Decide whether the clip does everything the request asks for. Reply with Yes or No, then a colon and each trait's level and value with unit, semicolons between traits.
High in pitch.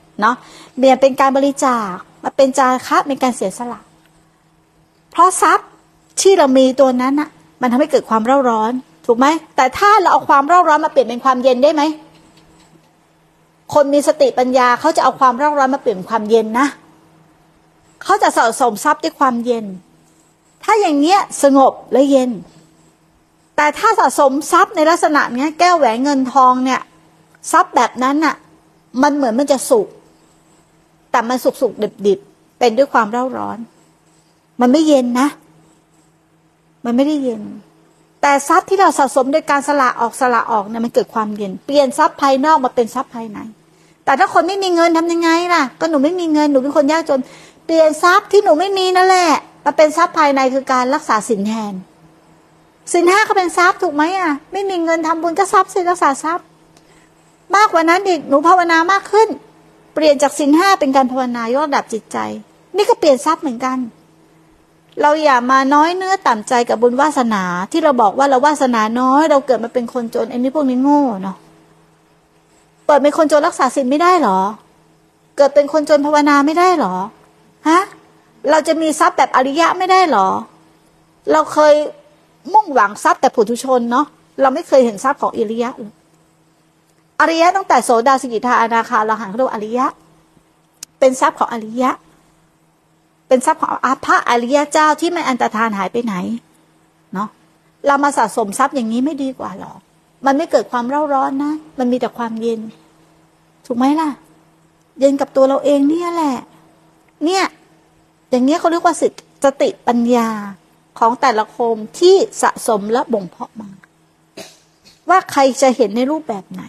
Yes: very high, 275 Hz